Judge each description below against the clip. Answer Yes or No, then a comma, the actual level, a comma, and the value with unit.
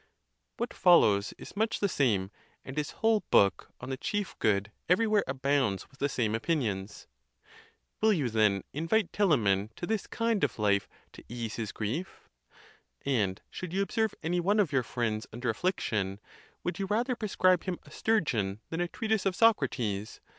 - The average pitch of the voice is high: No, medium, 140 Hz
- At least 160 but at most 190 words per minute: Yes, average, 175 wpm